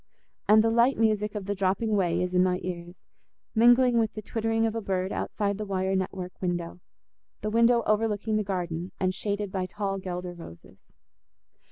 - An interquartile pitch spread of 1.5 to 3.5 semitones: Yes, average, 3.1 semitones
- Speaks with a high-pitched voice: Yes, high, 200 Hz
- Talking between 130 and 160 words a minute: No, average, 175 wpm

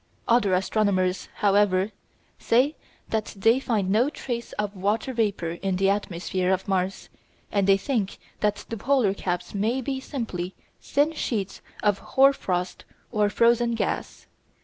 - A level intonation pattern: No, average, 3.6 semitones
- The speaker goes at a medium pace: Yes, average, 145 wpm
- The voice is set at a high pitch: Yes, high, 205 Hz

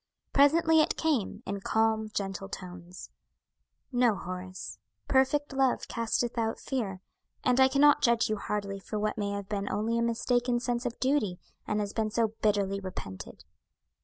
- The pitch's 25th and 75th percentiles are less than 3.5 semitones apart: No, average, 3.8 semitones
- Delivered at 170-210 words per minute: No, average, 160 wpm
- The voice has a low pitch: No, high, 220 Hz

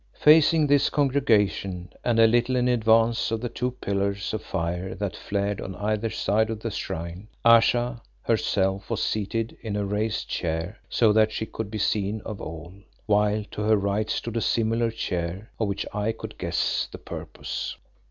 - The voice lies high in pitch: No, low, 110 Hz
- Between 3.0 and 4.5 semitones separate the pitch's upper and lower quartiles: No, narrow, 2.5 semitones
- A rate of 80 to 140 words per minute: No, average, 175 wpm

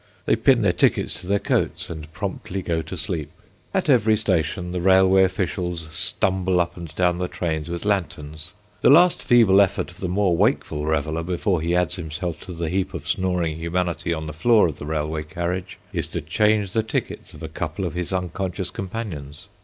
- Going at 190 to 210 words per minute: Yes, average, 195 wpm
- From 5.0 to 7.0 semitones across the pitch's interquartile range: No, average, 3.0 semitones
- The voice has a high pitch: No, very low, 90 Hz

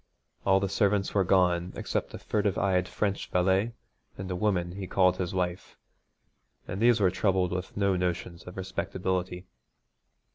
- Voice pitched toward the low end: Yes, very low, 95 Hz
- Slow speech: No, average, 155 wpm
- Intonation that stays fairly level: Yes, narrow, 1.5 semitones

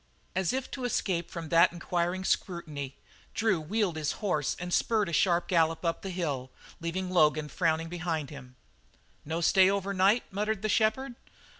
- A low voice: No, medium, 175 Hz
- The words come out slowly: No, average, 165 wpm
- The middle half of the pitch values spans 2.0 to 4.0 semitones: Yes, average, 3.5 semitones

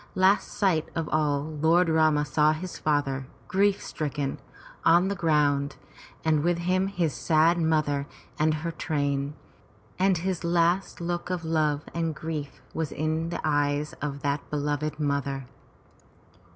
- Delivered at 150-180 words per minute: No, average, 140 wpm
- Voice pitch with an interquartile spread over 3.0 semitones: No, narrow, 2.6 semitones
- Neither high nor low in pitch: Yes, medium, 155 Hz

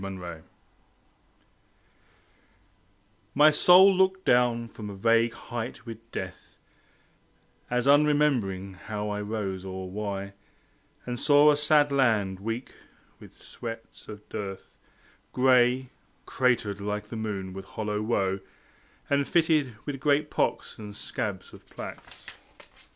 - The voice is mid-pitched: No, low, 115 Hz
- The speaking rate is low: Yes, slow, 120 wpm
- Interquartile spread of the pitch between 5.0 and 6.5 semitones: Yes, wide, 5.5 semitones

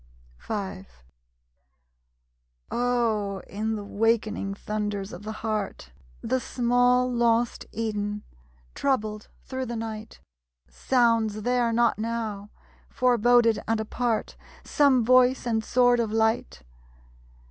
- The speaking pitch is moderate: No, high, 225 Hz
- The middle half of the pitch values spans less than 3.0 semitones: Yes, narrow, 2.4 semitones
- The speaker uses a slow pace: Yes, slow, 105 wpm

